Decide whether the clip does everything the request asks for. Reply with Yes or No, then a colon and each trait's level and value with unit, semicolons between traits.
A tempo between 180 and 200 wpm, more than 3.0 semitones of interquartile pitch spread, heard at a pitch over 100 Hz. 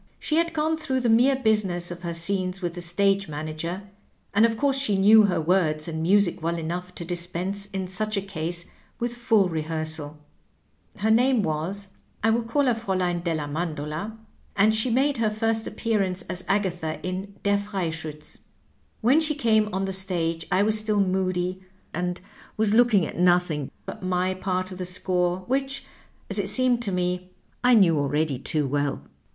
Yes: average, 185 wpm; average, 4.1 semitones; medium, 185 Hz